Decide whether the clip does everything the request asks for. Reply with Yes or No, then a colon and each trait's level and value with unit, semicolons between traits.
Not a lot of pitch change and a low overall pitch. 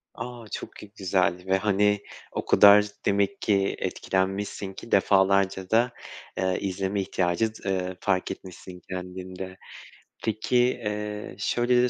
Yes: narrow, 2.0 semitones; low, 100 Hz